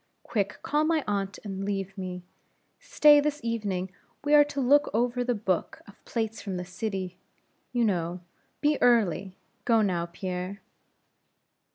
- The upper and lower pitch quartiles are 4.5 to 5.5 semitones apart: Yes, average, 4.9 semitones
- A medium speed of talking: Yes, average, 150 wpm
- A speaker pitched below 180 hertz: No, high, 205 Hz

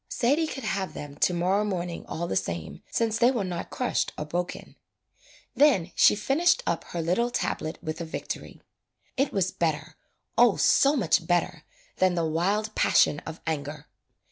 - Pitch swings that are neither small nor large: No, wide, 5.7 semitones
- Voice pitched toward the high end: No, medium, 180 Hz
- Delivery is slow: No, average, 170 wpm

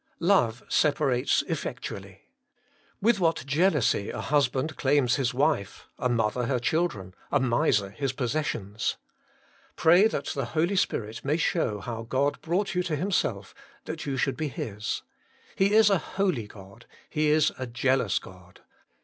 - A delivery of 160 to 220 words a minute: No, average, 150 wpm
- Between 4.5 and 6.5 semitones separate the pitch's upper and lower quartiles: Yes, wide, 5.6 semitones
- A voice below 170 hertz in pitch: Yes, low, 135 Hz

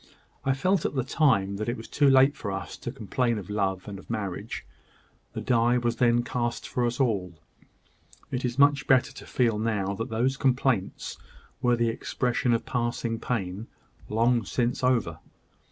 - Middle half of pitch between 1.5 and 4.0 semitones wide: Yes, average, 3.1 semitones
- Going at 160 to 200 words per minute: Yes, average, 175 wpm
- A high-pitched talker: No, low, 120 Hz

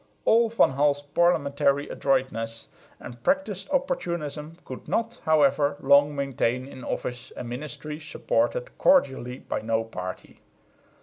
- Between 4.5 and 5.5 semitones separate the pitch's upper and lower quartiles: Yes, average, 5.0 semitones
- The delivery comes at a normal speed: No, slow, 120 wpm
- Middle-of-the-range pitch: Yes, medium, 145 Hz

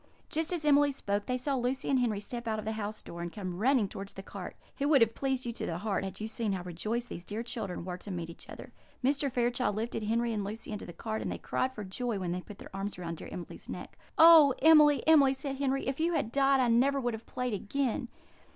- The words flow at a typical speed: No, fast, 260 wpm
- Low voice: No, high, 235 Hz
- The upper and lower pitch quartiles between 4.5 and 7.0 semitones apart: Yes, average, 5.0 semitones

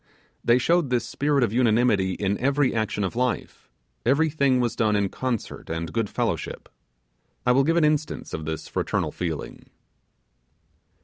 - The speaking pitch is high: No, low, 120 Hz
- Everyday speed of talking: Yes, average, 150 wpm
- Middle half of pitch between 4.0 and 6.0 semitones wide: Yes, average, 5.2 semitones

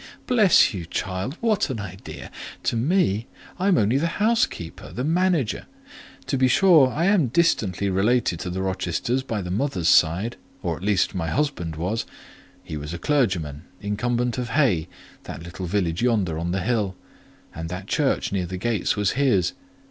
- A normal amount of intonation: No, wide, 7.1 semitones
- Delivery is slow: No, average, 165 wpm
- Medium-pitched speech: No, low, 105 Hz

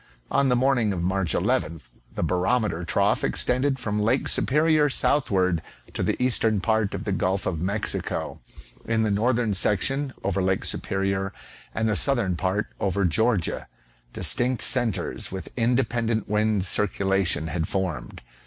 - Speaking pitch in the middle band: No, low, 105 Hz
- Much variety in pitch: No, average, 4.4 semitones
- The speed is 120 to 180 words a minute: Yes, average, 145 wpm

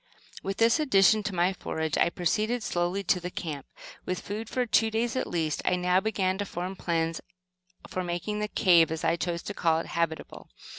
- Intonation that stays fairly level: No, average, 3.8 semitones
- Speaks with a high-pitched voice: No, medium, 180 Hz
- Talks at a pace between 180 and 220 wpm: Yes, average, 200 wpm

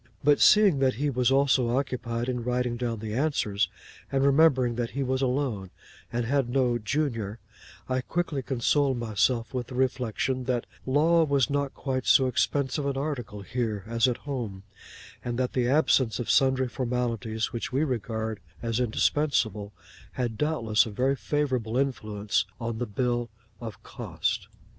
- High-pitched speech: No, low, 125 Hz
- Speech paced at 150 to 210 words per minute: Yes, average, 155 wpm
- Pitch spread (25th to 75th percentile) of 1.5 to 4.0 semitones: Yes, average, 2.9 semitones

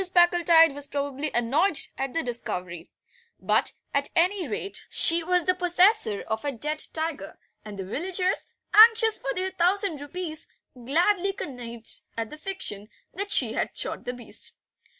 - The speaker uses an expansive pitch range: Yes, wide, 6.8 semitones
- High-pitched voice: Yes, very high, 315 Hz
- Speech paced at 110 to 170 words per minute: Yes, average, 150 wpm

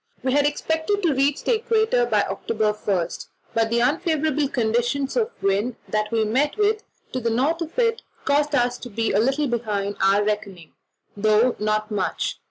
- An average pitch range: No, wide, 6.1 semitones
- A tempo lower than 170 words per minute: No, average, 180 wpm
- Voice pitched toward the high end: Yes, high, 245 Hz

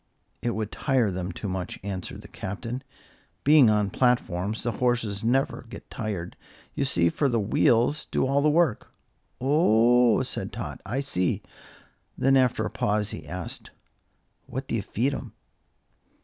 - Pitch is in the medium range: No, low, 115 Hz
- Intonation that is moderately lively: Yes, average, 4.7 semitones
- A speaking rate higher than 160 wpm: No, average, 155 wpm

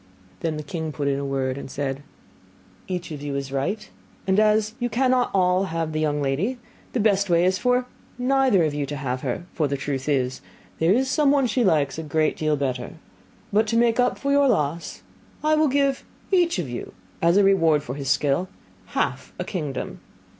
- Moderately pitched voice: Yes, medium, 170 Hz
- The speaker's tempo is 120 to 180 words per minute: No, average, 200 wpm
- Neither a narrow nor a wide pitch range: No, wide, 7.9 semitones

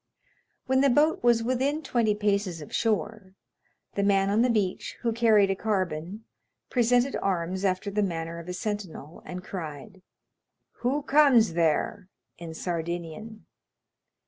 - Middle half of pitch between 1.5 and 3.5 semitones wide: No, average, 4.5 semitones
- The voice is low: No, high, 200 Hz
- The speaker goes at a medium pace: Yes, average, 145 wpm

